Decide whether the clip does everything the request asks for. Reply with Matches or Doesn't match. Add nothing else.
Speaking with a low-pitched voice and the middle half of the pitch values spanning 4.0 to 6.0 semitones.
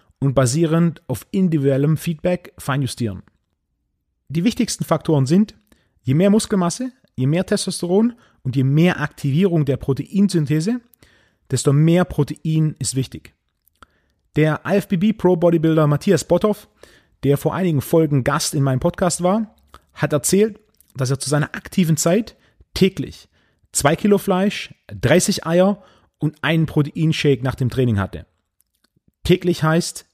Doesn't match